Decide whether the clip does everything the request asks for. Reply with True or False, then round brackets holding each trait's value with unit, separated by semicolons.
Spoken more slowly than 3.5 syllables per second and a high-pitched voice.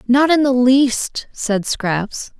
True (2.8 syllables/s; 250 Hz)